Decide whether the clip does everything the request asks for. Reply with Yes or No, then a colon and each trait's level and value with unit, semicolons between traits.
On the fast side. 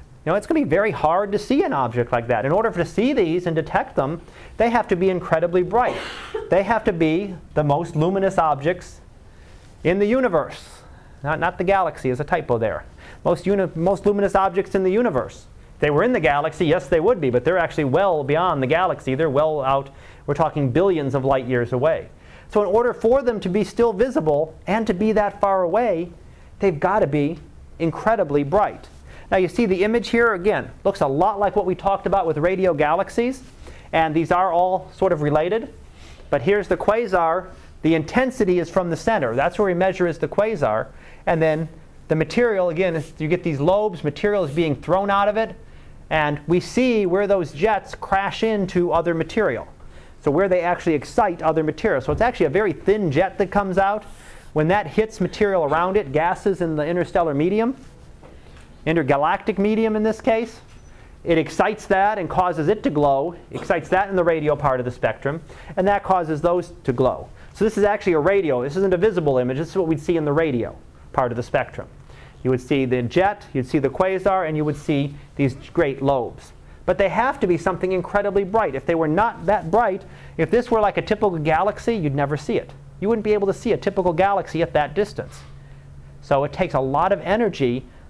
Yes: fast, 210 wpm